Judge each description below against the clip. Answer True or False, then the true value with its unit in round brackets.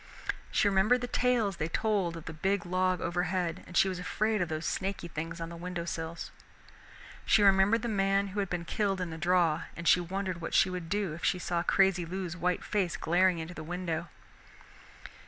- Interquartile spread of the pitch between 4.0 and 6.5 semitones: False (2.5 semitones)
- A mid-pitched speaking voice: True (180 Hz)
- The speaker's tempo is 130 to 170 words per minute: False (200 wpm)